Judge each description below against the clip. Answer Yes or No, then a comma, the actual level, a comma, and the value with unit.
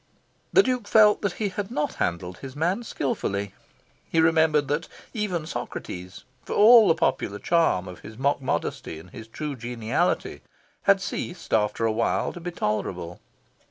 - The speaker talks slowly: No, average, 160 wpm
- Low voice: No, medium, 150 Hz